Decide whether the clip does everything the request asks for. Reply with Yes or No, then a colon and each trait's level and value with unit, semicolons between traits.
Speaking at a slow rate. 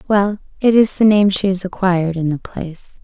No: average, 200 wpm